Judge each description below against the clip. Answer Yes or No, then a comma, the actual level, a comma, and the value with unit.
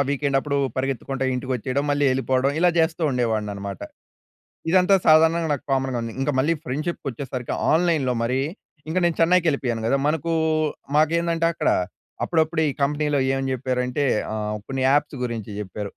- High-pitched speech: No, medium, 140 Hz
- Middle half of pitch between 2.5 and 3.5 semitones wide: No, average, 4.2 semitones